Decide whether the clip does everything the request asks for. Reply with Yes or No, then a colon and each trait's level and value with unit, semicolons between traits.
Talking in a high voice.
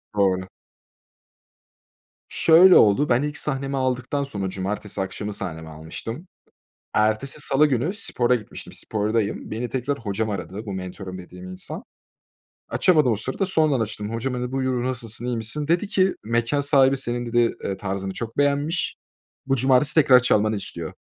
No: low, 120 Hz